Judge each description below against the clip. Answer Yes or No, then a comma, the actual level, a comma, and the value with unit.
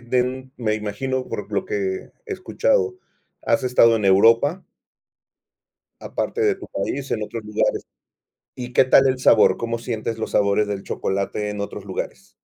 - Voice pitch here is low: Yes, low, 120 Hz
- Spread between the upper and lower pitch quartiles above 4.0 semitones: Yes, average, 4.4 semitones